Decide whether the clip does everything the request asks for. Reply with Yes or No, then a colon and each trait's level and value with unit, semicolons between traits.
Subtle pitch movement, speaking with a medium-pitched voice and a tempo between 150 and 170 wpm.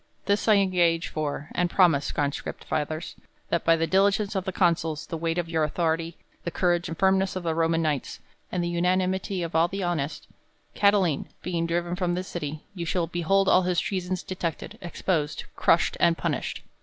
No: narrow, 2.1 semitones; medium, 175 Hz; average, 195 wpm